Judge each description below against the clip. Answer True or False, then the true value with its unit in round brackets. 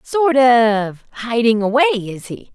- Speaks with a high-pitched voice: True (240 Hz)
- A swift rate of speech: False (140 wpm)